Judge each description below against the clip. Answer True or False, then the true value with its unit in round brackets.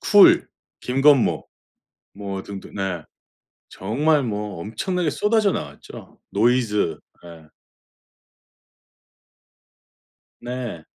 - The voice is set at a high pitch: False (110 Hz)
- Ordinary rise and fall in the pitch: False (6.7 semitones)